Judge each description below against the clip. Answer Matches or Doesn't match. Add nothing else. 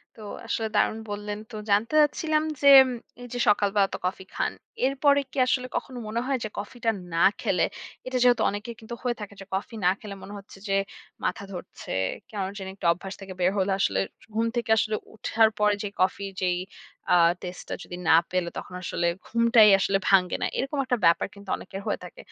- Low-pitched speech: Doesn't match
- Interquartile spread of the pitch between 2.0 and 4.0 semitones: Matches